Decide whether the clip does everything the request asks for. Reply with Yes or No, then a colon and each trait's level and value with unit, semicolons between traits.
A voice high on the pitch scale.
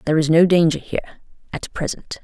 No: medium, 165 Hz